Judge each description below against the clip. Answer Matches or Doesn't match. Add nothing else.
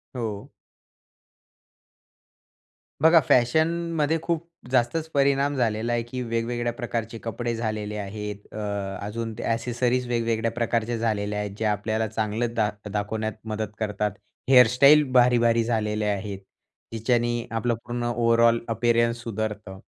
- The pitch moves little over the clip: Matches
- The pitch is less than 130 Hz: Matches